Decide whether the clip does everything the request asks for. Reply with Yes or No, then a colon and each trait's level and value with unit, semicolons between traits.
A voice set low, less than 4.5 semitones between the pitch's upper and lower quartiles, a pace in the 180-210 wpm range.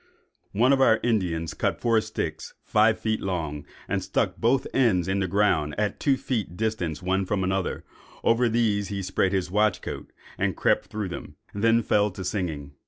Yes: low, 100 Hz; average, 3.4 semitones; average, 185 wpm